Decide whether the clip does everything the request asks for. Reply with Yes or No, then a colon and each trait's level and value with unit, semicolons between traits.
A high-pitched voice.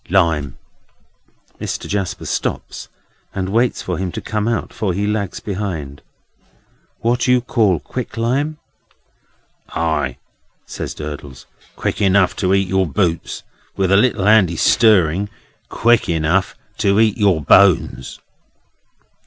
No: very low, 95 Hz